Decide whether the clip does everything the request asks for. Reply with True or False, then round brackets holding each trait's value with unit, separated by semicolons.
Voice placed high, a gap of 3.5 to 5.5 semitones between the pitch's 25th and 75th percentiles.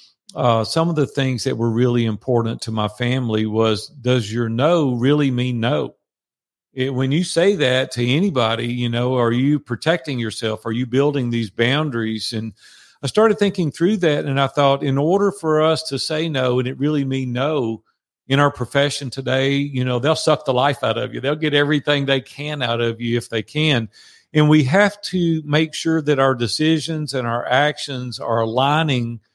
False (135 Hz; 4.1 semitones)